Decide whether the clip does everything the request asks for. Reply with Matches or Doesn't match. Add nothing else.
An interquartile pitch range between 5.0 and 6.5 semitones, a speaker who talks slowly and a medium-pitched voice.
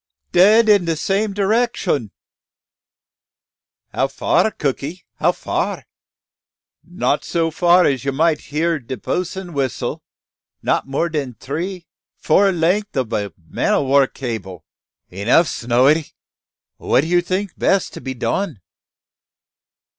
Matches